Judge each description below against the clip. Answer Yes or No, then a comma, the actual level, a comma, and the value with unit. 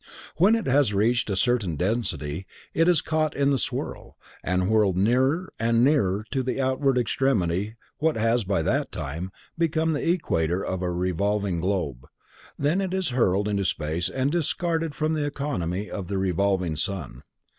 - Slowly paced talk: No, average, 170 wpm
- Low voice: Yes, low, 110 Hz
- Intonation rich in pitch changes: Yes, wide, 7.6 semitones